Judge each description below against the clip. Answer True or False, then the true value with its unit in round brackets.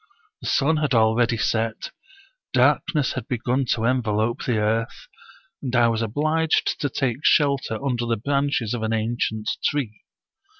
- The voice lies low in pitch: True (120 Hz)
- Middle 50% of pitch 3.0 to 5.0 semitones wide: True (3.7 semitones)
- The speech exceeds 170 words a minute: False (145 wpm)